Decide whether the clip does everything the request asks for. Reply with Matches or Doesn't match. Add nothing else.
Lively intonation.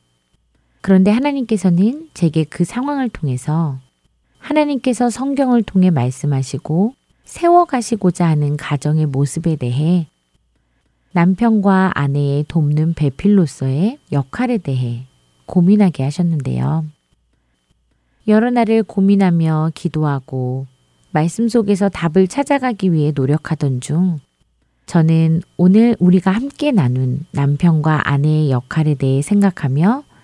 Matches